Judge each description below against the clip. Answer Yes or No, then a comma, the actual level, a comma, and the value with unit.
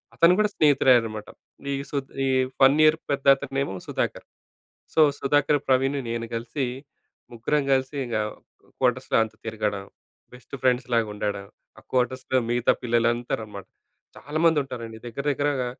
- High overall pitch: No, low, 125 Hz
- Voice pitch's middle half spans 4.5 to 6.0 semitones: No, average, 3.3 semitones